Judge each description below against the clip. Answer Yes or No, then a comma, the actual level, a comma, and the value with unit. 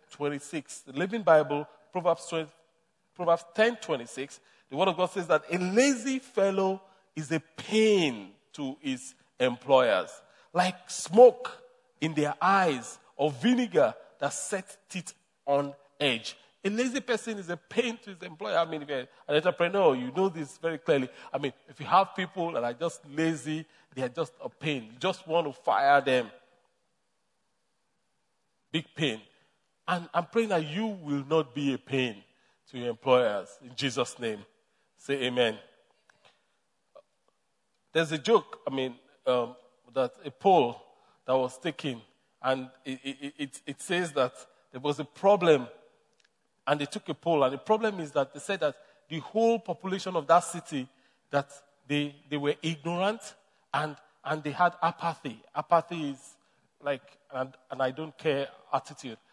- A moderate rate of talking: Yes, average, 160 wpm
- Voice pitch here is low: No, medium, 155 Hz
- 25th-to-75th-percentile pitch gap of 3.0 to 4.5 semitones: No, average, 5.2 semitones